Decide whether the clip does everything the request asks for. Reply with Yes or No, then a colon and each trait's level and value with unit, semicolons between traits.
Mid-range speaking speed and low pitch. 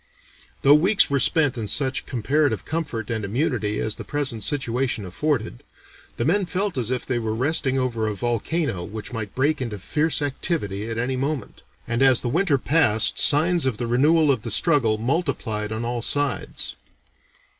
Yes: average, 175 wpm; low, 130 Hz